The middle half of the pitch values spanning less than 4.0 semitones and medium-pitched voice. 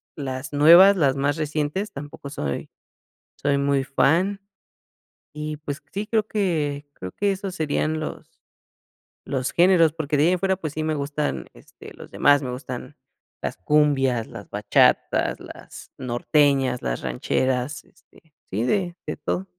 Yes: average, 3.6 semitones; medium, 150 Hz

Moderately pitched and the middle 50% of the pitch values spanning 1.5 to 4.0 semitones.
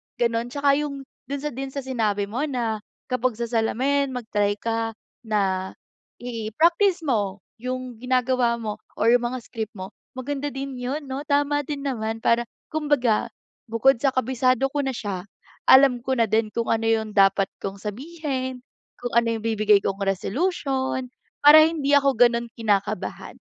No: high, 245 Hz; average, 3.7 semitones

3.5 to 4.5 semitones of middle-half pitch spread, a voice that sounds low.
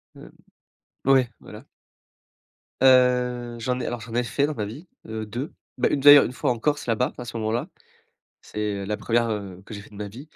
No: average, 3.0 semitones; low, 120 Hz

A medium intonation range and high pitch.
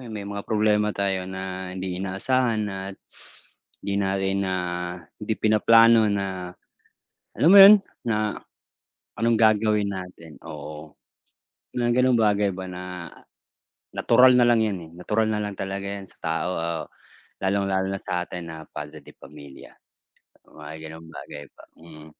No: average, 3.4 semitones; very low, 95 Hz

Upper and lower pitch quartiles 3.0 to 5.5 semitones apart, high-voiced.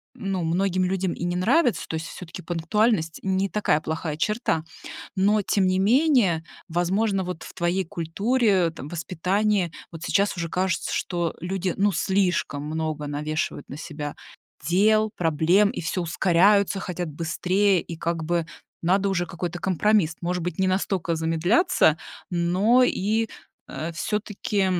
No: average, 3.3 semitones; medium, 180 Hz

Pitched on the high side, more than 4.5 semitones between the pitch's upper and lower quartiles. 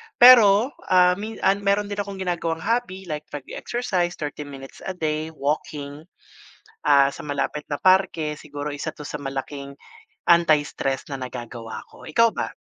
No: medium, 155 Hz; average, 5.0 semitones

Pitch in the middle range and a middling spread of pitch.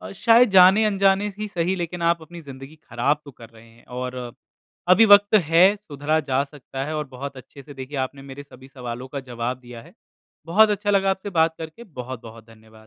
No: medium, 145 Hz; wide, 7.0 semitones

